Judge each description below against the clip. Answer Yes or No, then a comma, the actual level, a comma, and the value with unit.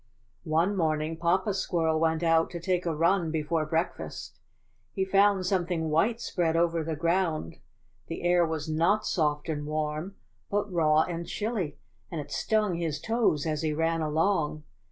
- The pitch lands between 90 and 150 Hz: No, medium, 165 Hz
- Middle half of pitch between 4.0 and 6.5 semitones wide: No, average, 2.8 semitones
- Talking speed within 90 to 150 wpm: No, average, 165 wpm